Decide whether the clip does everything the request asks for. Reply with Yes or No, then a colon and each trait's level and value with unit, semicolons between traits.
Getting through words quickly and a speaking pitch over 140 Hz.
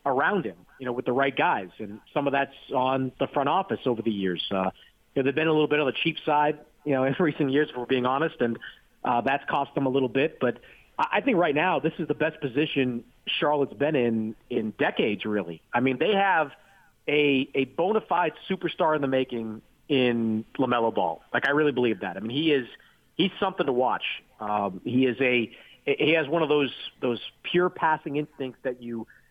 No: fast, 220 wpm; low, 135 Hz